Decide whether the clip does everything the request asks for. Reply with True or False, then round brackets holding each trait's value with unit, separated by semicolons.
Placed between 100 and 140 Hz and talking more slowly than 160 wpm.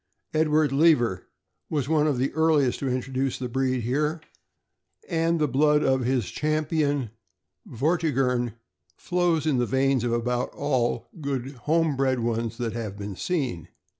True (135 Hz; 150 wpm)